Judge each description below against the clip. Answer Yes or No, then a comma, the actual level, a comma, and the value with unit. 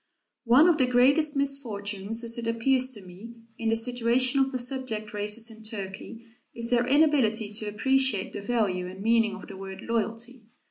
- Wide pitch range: No, average, 3.4 semitones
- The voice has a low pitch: No, high, 230 Hz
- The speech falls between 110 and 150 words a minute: No, average, 180 wpm